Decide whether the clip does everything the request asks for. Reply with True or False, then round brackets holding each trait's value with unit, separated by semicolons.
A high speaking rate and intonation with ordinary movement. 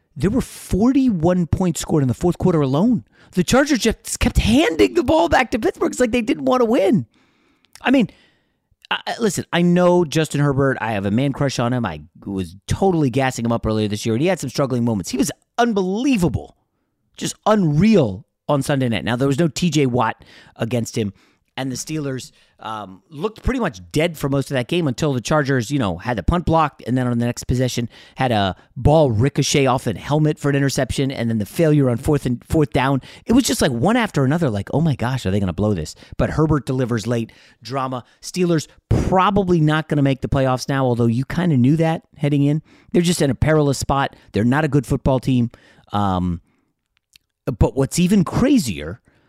False (215 wpm; 6.1 semitones)